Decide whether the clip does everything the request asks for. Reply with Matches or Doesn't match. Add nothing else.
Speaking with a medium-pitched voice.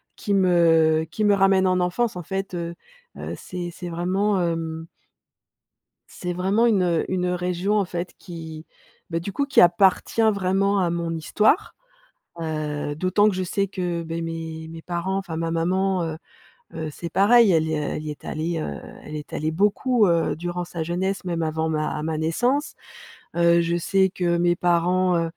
Matches